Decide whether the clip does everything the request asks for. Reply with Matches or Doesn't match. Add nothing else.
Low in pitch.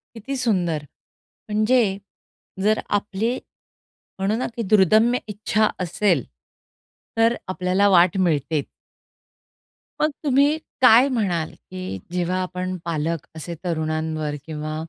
Doesn't match